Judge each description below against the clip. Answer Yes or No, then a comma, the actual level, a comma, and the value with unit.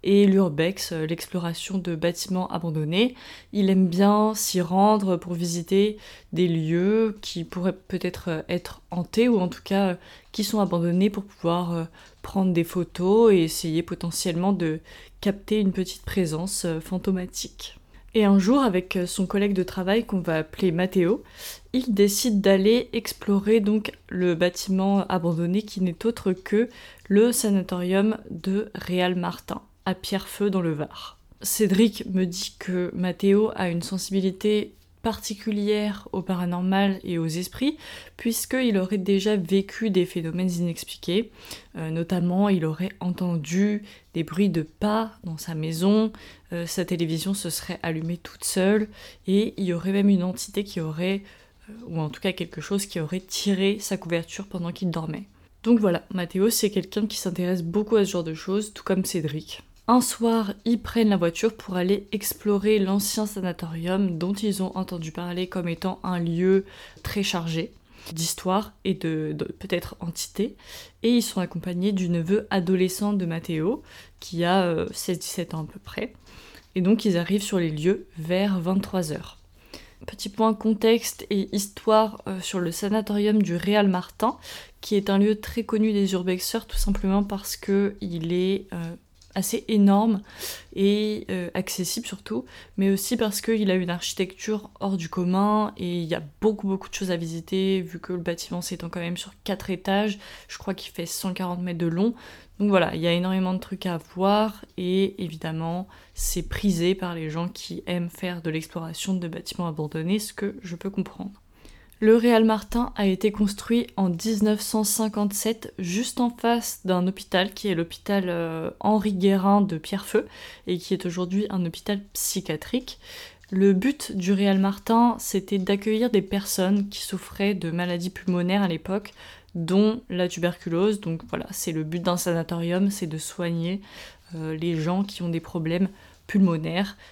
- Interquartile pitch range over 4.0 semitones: No, average, 2.7 semitones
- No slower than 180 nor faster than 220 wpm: No, average, 165 wpm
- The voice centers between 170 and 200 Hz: Yes, high, 190 Hz